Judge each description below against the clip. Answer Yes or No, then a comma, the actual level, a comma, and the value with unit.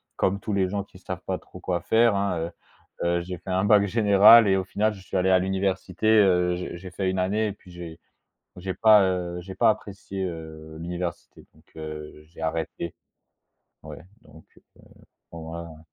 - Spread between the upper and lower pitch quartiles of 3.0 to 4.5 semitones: No, narrow, 2.5 semitones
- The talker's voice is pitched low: Yes, very low, 95 Hz